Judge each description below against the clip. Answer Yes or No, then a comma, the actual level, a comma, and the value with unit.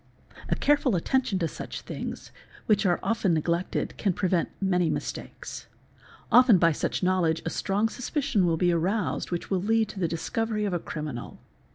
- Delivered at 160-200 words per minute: Yes, average, 170 wpm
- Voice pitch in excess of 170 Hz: Yes, medium, 185 Hz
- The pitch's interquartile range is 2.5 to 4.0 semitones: No, average, 4.6 semitones